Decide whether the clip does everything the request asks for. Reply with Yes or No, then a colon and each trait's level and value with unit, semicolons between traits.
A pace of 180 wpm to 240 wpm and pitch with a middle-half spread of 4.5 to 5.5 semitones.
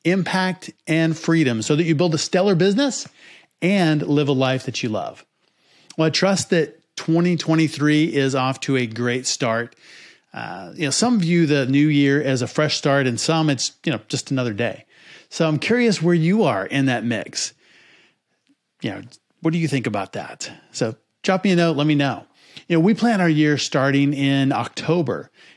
No: average, 190 wpm; average, 4.1 semitones